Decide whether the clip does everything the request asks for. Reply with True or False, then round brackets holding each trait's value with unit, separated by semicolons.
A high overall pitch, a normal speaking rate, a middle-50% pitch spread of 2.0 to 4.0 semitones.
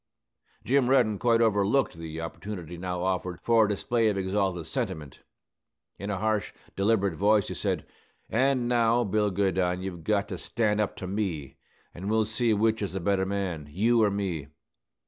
False (100 Hz; 170 wpm; 3.3 semitones)